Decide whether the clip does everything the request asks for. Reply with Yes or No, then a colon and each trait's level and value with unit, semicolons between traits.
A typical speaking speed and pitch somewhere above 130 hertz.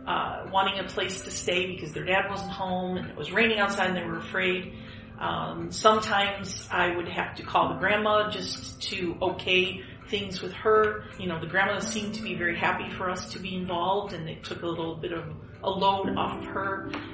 No: fast, 215 wpm; high, 190 Hz